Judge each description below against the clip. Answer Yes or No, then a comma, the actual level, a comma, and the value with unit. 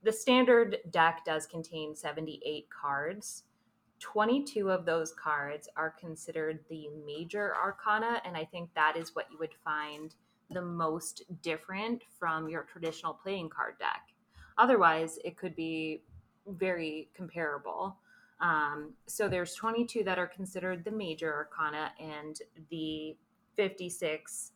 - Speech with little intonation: No, average, 3.6 semitones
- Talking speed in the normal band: No, slow, 130 wpm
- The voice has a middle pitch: Yes, medium, 165 Hz